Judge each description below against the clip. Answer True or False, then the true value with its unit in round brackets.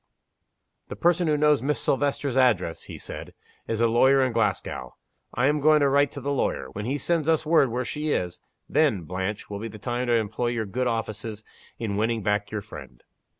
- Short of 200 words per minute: False (205 wpm)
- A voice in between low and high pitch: False (120 Hz)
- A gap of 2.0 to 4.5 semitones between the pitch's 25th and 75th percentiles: False (5.2 semitones)